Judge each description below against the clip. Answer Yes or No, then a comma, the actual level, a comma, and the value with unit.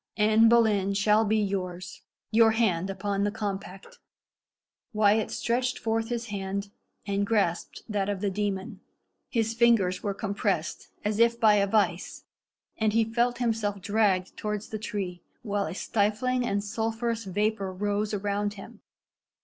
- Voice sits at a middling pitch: No, high, 210 Hz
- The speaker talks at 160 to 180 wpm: No, average, 145 wpm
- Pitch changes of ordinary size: No, narrow, 2.2 semitones